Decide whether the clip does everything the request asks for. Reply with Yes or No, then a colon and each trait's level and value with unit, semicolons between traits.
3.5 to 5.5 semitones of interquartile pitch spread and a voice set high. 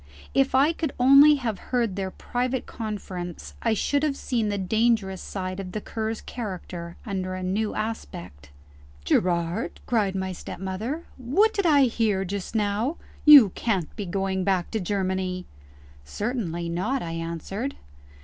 Yes: average, 4.7 semitones; high, 205 Hz